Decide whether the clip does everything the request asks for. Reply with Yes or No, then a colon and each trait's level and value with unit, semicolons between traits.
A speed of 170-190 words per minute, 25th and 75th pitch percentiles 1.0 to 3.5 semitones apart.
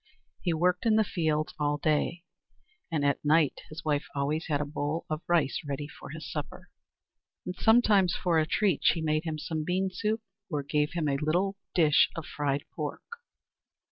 Yes: average, 185 wpm; average, 3.1 semitones